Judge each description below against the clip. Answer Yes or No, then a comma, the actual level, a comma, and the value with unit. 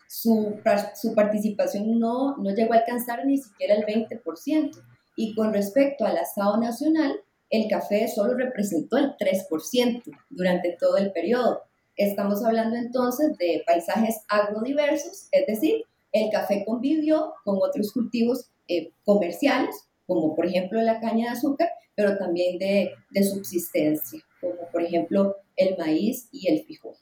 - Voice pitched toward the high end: Yes, high, 220 Hz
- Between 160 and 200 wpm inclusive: No, average, 140 wpm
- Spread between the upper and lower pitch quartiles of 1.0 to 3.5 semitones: No, average, 4.8 semitones